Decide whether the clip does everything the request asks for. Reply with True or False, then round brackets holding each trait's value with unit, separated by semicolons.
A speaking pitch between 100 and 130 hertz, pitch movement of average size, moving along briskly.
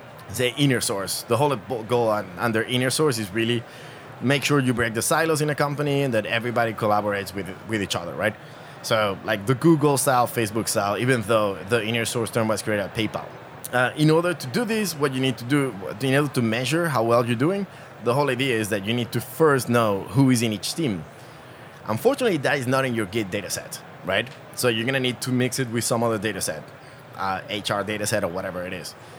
True (120 Hz; 3.7 semitones; 230 wpm)